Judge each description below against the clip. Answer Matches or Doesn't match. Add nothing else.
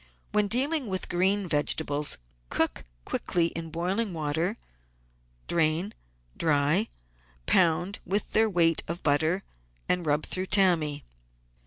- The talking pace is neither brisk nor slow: Doesn't match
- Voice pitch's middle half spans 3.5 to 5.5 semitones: Matches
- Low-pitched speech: Doesn't match